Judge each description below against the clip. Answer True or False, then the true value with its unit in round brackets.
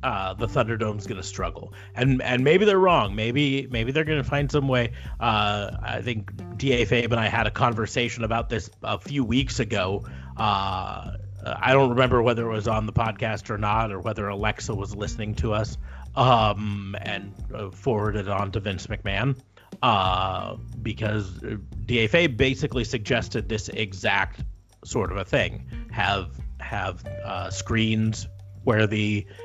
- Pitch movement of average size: True (3.2 semitones)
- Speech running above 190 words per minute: False (160 wpm)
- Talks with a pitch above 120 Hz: False (110 Hz)